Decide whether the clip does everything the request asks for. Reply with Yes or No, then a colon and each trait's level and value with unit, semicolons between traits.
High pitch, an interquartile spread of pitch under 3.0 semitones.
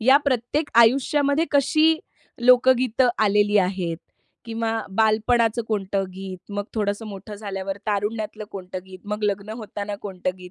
No: high, 215 Hz; average, 3.5 semitones